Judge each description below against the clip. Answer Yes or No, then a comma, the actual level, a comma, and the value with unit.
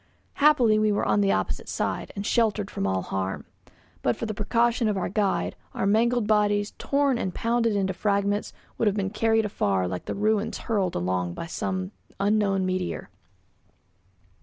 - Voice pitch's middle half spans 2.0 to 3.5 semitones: Yes, average, 2.9 semitones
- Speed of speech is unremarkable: Yes, average, 170 wpm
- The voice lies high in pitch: Yes, high, 205 Hz